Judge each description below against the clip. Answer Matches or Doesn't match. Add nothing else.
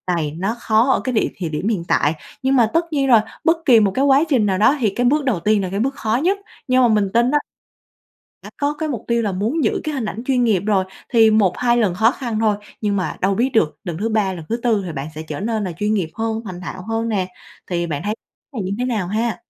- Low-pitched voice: Doesn't match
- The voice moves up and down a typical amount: Matches